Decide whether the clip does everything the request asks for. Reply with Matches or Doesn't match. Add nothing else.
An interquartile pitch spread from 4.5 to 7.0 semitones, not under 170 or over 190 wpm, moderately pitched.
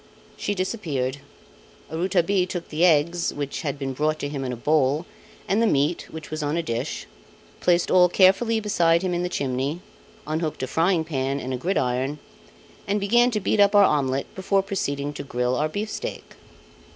Matches